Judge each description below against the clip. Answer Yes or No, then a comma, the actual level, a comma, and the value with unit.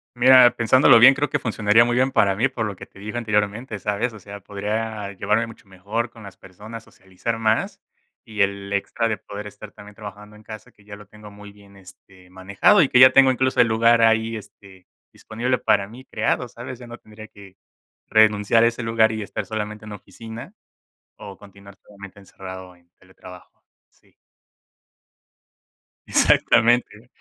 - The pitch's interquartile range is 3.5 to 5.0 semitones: No, narrow, 2.5 semitones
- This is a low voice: Yes, low, 105 Hz